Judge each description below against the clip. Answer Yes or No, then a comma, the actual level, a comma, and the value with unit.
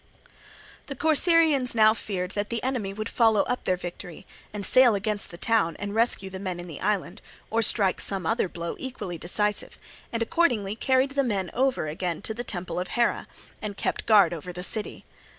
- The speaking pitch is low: No, high, 210 Hz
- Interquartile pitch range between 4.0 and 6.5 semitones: Yes, average, 4.5 semitones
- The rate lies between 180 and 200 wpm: Yes, average, 190 wpm